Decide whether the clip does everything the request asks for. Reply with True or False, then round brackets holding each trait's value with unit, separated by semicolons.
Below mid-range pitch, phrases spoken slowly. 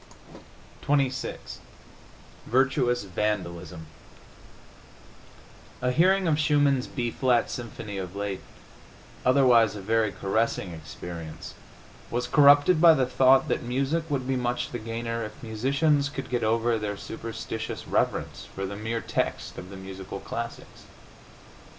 True (120 Hz; 125 wpm)